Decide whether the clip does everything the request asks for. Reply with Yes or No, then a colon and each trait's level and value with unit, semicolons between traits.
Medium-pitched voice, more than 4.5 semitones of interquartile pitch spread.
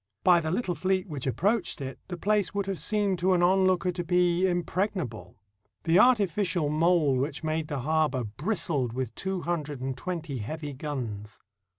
Yes: medium, 170 Hz; average, 4.9 semitones